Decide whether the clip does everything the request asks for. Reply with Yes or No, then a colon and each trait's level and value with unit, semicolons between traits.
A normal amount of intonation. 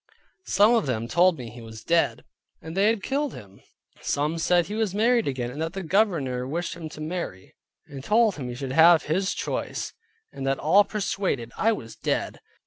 No: wide, 7.2 semitones